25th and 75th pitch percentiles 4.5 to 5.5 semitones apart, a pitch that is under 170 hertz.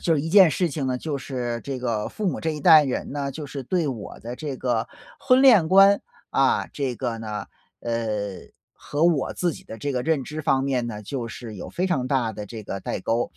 Yes: average, 5.0 semitones; low, 135 Hz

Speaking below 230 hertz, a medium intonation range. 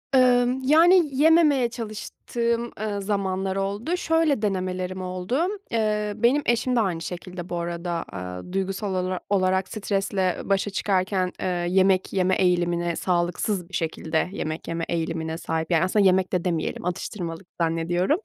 Yes: high, 190 Hz; average, 3.5 semitones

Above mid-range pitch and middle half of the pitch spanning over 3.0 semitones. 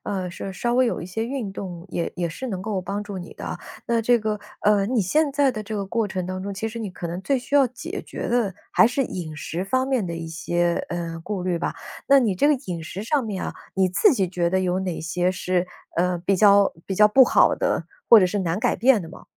Yes: high, 195 Hz; average, 4.5 semitones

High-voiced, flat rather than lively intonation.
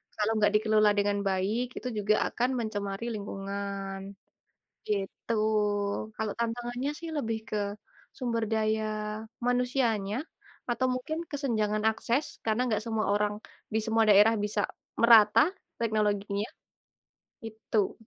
Yes: high, 215 Hz; narrow, 2.2 semitones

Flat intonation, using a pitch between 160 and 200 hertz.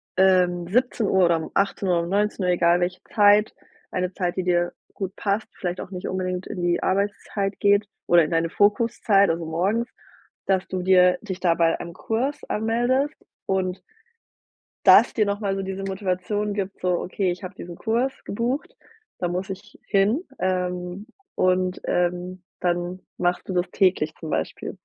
Yes: narrow, 2.3 semitones; medium, 185 Hz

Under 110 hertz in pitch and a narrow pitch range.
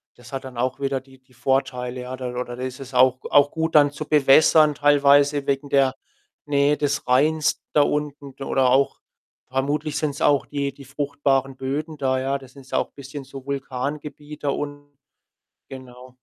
No: medium, 140 Hz; narrow, 1.8 semitones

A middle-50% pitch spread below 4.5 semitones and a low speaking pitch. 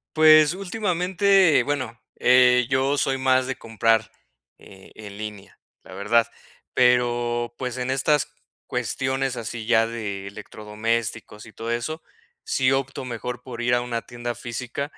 Yes: average, 2.9 semitones; low, 125 Hz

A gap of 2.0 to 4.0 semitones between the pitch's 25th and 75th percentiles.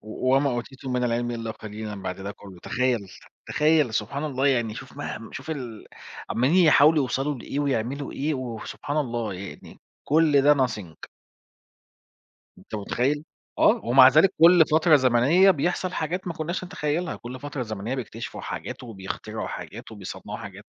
No: average, 4.7 semitones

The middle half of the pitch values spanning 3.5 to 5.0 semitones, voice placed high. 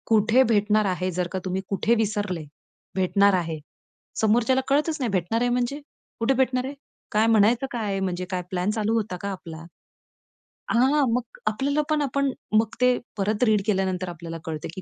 Yes: average, 4.7 semitones; high, 215 Hz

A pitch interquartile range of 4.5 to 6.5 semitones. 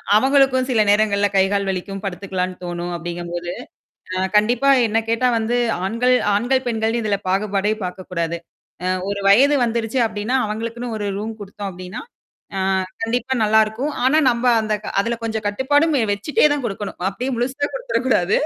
No: average, 4.1 semitones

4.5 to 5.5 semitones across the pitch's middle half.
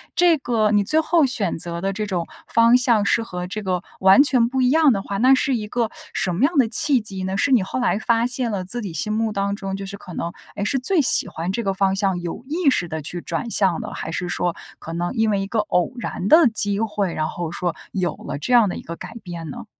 Yes: average, 5.0 semitones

